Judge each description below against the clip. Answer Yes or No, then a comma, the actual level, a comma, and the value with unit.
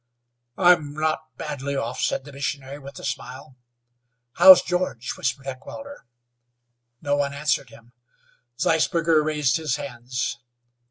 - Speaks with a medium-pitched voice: Yes, medium, 145 Hz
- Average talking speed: No, slow, 120 wpm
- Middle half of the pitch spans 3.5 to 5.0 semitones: No, average, 2.8 semitones